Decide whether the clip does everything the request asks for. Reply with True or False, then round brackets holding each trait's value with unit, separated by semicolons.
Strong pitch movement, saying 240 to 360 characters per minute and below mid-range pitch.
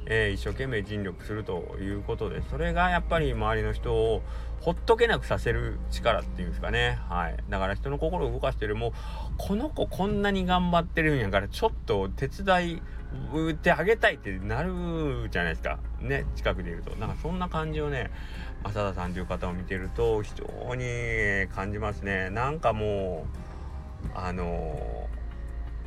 True (8.6 semitones; 350 characters per minute; 105 Hz)